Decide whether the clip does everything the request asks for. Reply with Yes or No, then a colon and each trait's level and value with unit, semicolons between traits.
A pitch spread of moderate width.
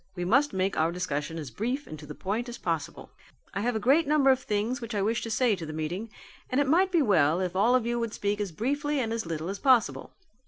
No: wide, 6.2 semitones